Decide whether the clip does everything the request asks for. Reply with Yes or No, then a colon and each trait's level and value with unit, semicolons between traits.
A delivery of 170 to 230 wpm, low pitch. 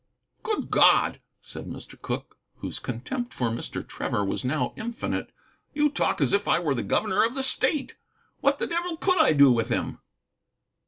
No: average, 175 wpm; high, 235 Hz